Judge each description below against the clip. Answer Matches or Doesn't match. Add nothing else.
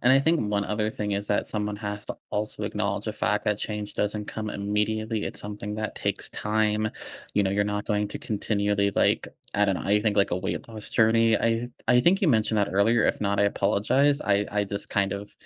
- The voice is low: Matches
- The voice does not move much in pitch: Matches